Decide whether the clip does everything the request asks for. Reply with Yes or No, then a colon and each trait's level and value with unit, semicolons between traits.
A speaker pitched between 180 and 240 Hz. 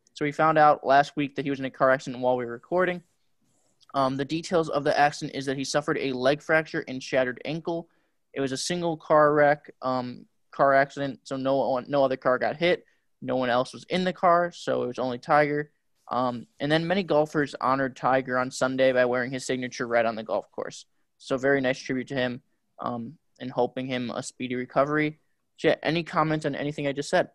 No: low, 135 Hz